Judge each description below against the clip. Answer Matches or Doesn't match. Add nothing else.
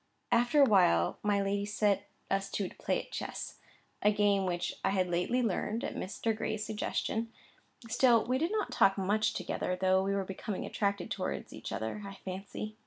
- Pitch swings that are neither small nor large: Doesn't match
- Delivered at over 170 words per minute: Matches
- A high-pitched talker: Matches